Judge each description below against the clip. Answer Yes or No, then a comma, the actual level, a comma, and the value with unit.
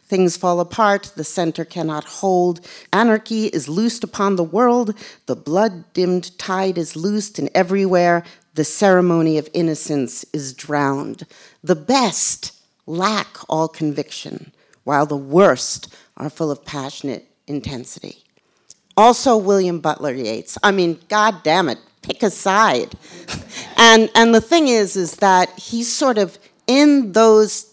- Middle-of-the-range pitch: Yes, medium, 180 Hz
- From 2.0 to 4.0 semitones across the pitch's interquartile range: No, wide, 5.5 semitones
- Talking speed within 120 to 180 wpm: Yes, average, 140 wpm